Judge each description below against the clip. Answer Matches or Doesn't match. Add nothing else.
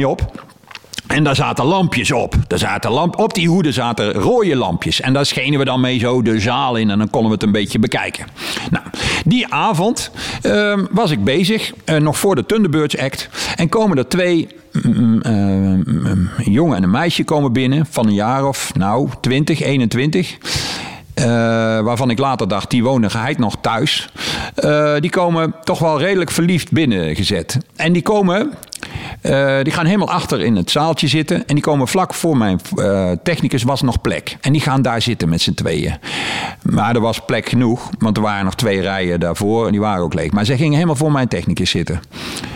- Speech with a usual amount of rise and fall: Doesn't match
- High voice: Doesn't match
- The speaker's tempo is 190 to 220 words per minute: Matches